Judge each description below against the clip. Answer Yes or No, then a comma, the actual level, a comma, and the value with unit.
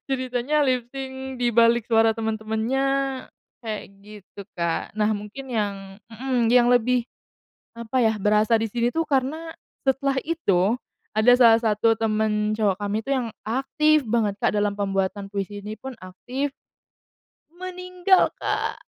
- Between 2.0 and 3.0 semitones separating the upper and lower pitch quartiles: No, average, 3.9 semitones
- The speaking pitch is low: No, high, 230 Hz